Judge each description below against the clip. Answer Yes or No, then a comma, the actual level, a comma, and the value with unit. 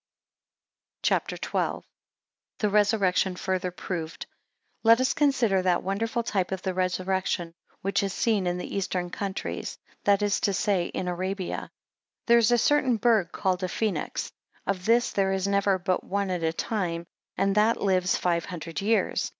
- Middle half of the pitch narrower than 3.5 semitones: Yes, narrow, 2.6 semitones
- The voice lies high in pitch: Yes, high, 195 Hz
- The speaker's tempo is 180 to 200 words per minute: No, average, 165 wpm